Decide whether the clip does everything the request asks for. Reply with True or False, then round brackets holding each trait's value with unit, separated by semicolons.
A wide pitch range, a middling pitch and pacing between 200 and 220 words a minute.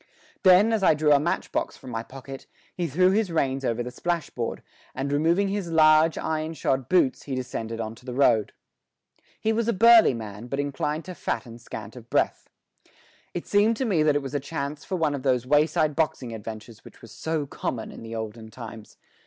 True (5.7 semitones; 145 Hz; 205 wpm)